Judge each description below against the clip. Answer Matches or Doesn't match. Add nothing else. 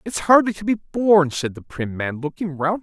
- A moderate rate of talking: Doesn't match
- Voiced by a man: Matches